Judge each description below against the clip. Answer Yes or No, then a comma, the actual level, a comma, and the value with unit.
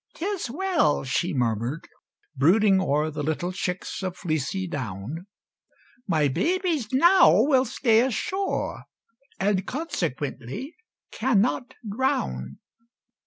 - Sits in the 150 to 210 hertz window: Yes, high, 190 Hz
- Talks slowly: Yes, slow, 100 wpm